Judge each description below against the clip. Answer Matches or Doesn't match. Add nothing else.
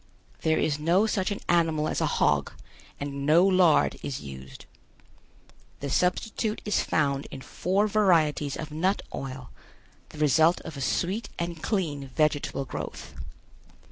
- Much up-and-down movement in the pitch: Doesn't match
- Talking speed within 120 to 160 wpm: Matches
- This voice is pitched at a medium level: Matches